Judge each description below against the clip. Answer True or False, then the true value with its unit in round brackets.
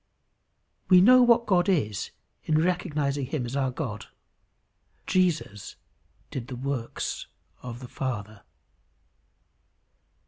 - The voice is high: False (140 Hz)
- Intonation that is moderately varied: False (6.9 semitones)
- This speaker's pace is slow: True (105 wpm)